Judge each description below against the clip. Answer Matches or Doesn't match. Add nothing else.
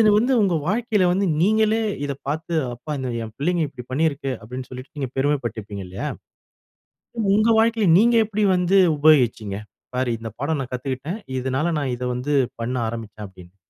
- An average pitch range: Doesn't match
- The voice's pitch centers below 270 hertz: Matches